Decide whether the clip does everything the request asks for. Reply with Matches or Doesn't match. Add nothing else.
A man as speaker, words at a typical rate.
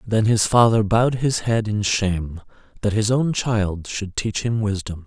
Matches